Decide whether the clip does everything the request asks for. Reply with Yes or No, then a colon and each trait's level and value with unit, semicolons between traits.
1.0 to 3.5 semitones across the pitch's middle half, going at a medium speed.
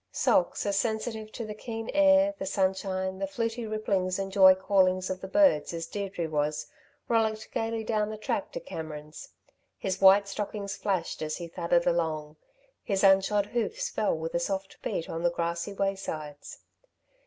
No: average, 3.9 semitones; average, 165 wpm